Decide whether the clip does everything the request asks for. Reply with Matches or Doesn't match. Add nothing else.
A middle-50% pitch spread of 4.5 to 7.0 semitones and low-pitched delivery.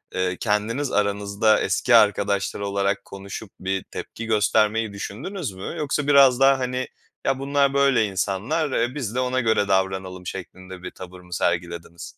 Matches